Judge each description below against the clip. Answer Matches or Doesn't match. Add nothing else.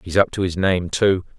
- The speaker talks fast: Matches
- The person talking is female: Doesn't match